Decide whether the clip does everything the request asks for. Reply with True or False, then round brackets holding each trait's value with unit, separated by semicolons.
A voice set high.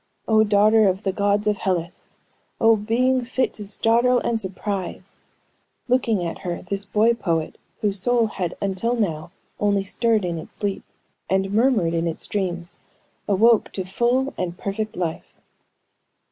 True (205 Hz)